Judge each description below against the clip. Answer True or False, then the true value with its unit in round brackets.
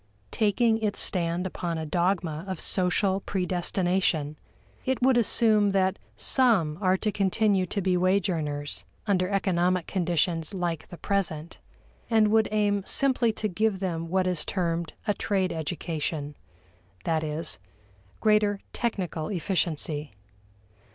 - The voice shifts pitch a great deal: False (3.5 semitones)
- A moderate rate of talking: False (130 wpm)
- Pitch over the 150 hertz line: True (185 Hz)